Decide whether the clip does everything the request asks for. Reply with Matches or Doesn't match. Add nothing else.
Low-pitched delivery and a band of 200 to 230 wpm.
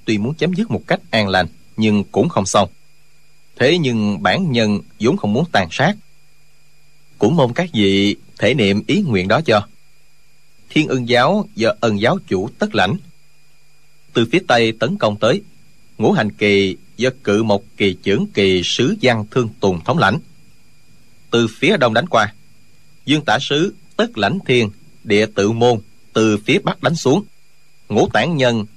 Doesn't match